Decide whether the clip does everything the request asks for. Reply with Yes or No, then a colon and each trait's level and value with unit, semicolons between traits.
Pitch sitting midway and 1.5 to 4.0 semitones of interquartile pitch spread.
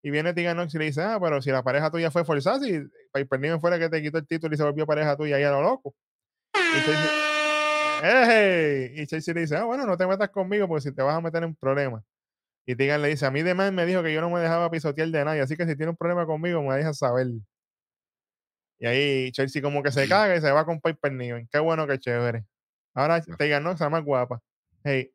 Yes: medium, 155 Hz; average, 3.7 semitones